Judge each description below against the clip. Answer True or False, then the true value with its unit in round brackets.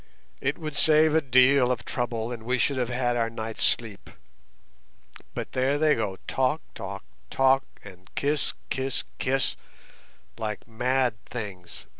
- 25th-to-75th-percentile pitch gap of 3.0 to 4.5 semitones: True (3.3 semitones)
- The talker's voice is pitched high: False (125 Hz)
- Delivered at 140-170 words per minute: True (145 wpm)